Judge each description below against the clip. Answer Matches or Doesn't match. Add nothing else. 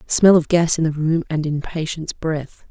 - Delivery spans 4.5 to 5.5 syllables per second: Doesn't match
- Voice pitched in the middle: Matches